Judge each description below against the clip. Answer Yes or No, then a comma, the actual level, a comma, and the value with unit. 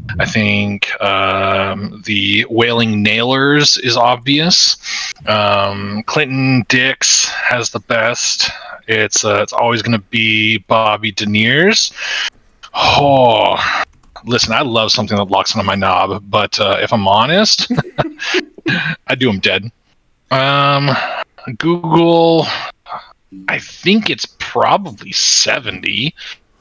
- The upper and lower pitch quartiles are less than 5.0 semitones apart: No, average, 5.3 semitones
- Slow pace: Yes, slow, 110 wpm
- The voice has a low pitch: Yes, low, 120 Hz